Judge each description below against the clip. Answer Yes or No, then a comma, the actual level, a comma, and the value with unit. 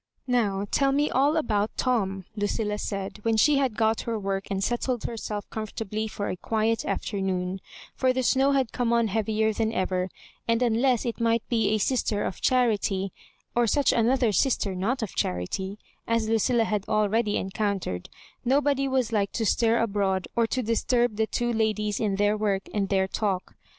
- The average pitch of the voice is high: Yes, high, 220 Hz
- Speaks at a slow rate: No, average, 180 wpm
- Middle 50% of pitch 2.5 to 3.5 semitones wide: Yes, average, 3.1 semitones